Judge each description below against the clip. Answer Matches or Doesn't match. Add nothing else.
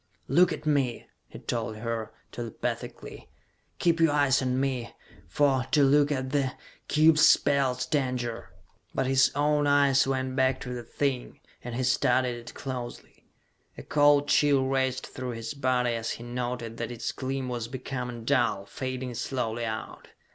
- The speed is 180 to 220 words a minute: Doesn't match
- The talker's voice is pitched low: Matches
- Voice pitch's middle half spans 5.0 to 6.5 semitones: Doesn't match